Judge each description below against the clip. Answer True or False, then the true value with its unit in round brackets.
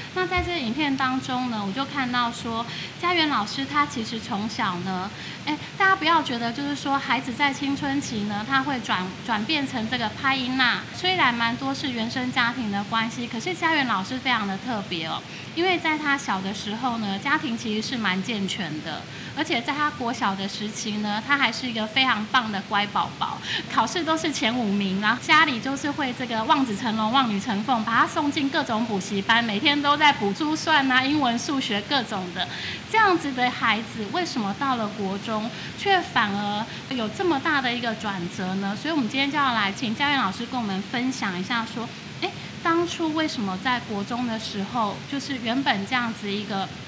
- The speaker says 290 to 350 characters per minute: True (300 characters per minute)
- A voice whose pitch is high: True (240 Hz)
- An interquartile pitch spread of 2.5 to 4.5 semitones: False (5.0 semitones)